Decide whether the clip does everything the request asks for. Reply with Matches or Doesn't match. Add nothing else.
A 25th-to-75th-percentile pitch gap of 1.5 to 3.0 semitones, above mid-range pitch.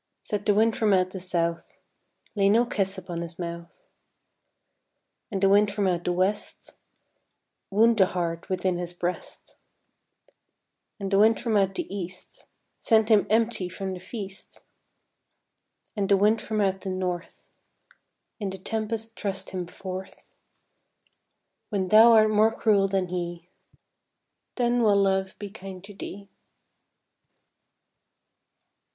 Matches